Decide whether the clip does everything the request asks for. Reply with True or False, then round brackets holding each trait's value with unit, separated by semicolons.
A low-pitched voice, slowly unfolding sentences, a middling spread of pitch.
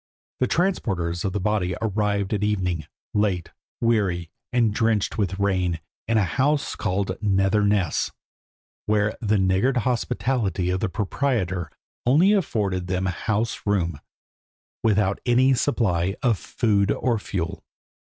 True (105 Hz; 130 wpm; 3.6 semitones)